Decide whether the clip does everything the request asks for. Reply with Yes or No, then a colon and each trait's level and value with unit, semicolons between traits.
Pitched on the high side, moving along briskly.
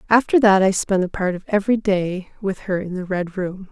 Yes: high, 195 Hz; fast, 240 wpm